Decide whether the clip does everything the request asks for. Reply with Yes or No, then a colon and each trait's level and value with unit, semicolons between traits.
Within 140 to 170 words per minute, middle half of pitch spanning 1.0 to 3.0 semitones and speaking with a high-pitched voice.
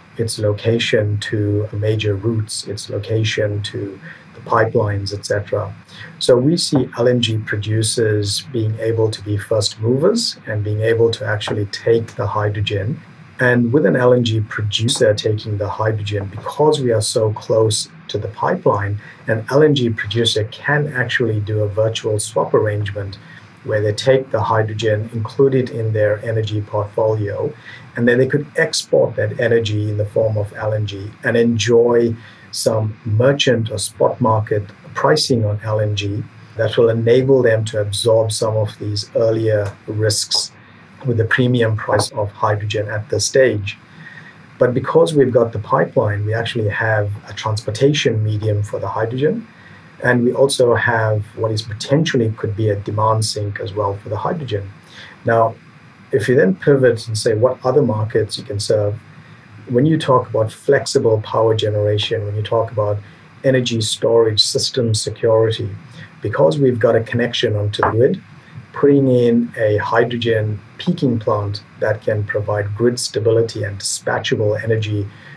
No: average, 150 wpm; narrow, 2.6 semitones; low, 110 Hz